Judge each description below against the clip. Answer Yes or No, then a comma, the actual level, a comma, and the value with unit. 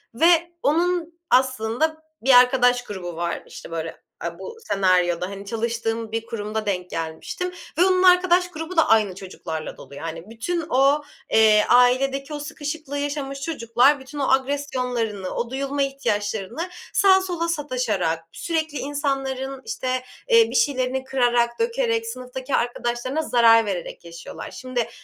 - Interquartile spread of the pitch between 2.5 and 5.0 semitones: No, wide, 5.4 semitones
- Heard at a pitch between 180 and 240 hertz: No, very high, 255 Hz